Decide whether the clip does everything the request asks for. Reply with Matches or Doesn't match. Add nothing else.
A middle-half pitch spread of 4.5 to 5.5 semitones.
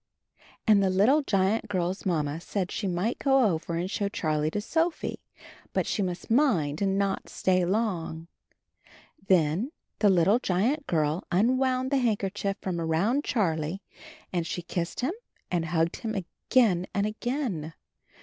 Matches